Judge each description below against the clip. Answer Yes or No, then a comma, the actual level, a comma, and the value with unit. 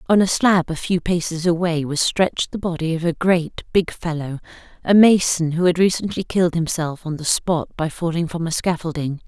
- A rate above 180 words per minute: Yes, average, 200 wpm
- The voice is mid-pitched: Yes, medium, 170 Hz